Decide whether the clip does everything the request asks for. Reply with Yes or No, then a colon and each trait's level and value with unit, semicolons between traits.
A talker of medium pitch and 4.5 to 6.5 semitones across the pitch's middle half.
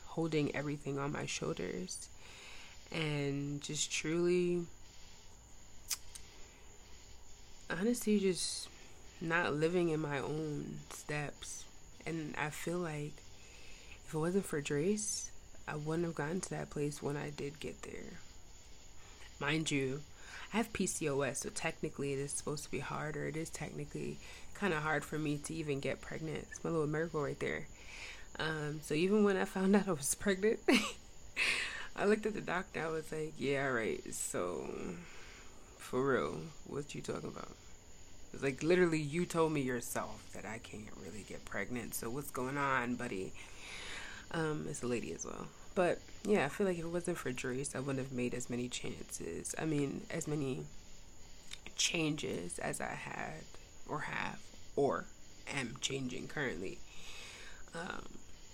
Yes: medium, 145 Hz; average, 5.1 semitones